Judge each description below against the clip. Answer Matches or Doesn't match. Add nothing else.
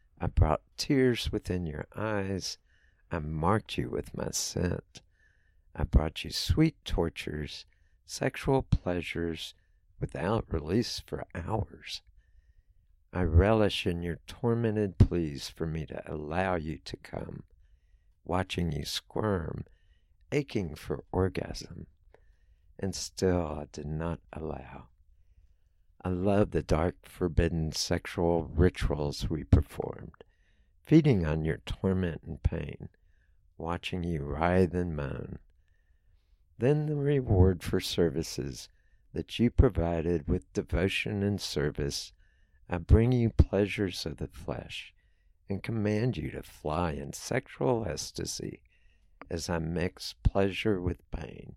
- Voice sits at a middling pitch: Doesn't match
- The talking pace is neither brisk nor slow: Doesn't match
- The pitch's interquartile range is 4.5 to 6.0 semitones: Doesn't match